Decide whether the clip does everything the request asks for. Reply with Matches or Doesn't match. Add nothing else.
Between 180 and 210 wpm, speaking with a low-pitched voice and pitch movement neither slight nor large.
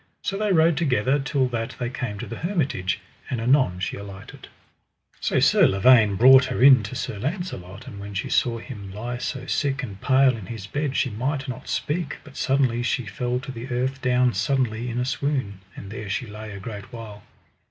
Matches